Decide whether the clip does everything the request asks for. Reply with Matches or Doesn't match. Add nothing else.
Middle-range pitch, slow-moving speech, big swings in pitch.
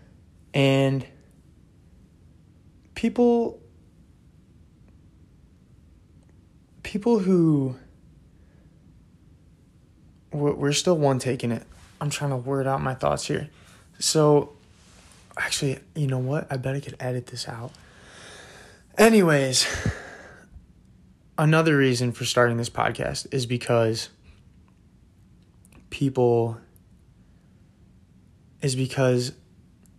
Doesn't match